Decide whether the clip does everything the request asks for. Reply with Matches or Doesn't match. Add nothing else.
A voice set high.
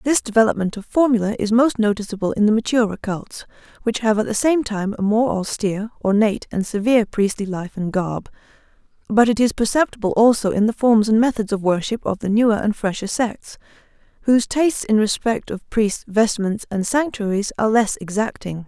Matches